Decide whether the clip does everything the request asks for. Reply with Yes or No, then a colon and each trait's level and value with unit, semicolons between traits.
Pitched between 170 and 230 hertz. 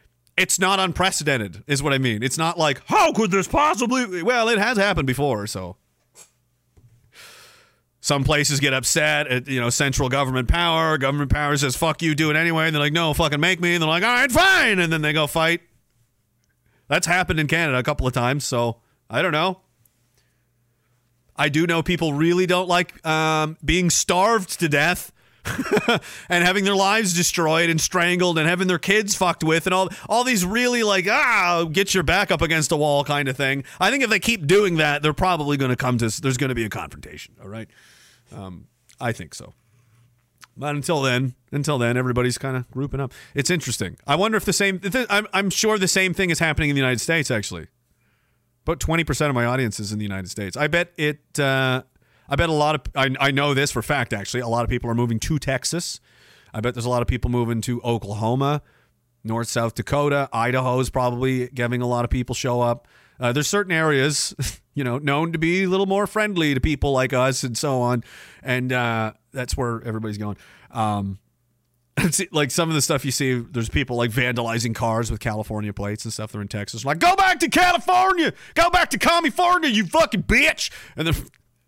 No: medium, 140 Hz